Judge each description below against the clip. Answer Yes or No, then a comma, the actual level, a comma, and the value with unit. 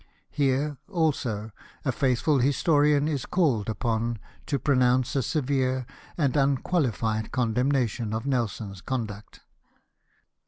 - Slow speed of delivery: Yes, slow, 110 wpm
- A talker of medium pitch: No, low, 130 Hz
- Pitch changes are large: No, average, 3.8 semitones